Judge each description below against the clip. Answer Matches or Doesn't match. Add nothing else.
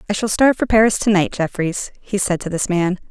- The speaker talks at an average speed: Doesn't match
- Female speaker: Matches